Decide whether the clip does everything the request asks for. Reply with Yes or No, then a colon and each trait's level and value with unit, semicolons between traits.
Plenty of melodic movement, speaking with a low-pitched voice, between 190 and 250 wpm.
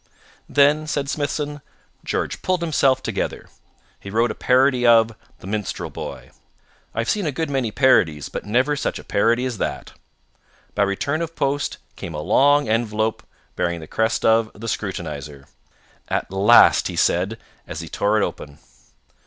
No: wide, 5.8 semitones; low, 115 Hz; average, 160 wpm